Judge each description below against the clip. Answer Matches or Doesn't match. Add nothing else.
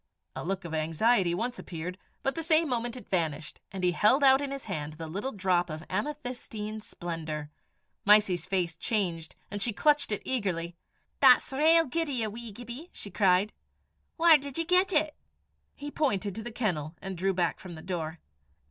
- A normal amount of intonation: Doesn't match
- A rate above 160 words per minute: Matches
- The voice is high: Matches